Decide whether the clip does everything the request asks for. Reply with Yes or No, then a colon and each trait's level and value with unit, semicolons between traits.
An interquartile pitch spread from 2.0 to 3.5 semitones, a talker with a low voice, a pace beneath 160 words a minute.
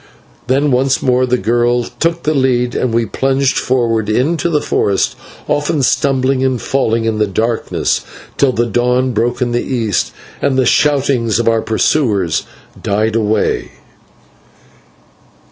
Yes: average, 2.9 semitones; low, 125 Hz; average, 145 wpm